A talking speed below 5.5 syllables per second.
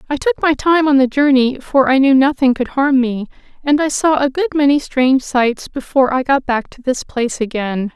Yes: 5.3 syllables/s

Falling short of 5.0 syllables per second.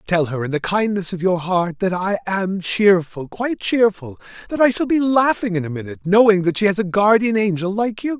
No: 5.4 syllables/s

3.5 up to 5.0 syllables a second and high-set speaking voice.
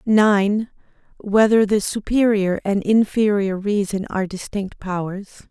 Yes: 4.5 syllables/s; high, 205 Hz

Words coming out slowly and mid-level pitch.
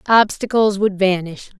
No: slow, 115 wpm; high, 200 Hz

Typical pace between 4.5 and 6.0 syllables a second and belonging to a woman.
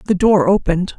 Yes: 5.4 syllables/s; female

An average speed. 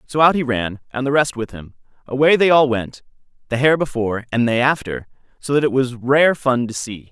No: fast, 220 wpm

